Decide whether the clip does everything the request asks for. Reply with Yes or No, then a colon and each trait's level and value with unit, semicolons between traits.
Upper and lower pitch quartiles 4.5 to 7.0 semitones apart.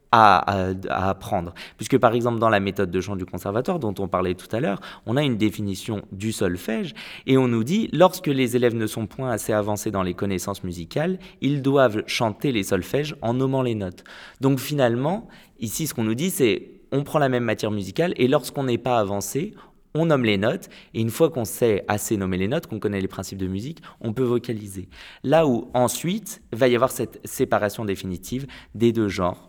Yes: average, 5.0 semitones